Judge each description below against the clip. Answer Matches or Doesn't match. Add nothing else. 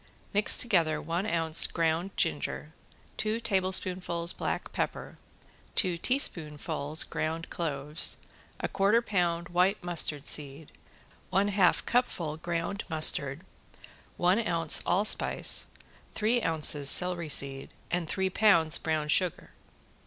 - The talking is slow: Matches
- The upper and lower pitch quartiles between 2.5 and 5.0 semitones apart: Matches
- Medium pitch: Matches